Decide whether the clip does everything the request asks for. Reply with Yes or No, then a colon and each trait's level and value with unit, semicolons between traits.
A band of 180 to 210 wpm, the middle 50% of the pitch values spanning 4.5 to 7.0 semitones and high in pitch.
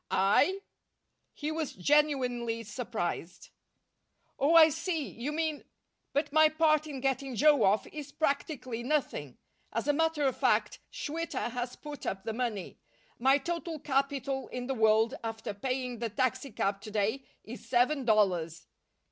No: average, 145 wpm; average, 4.9 semitones; very high, 265 Hz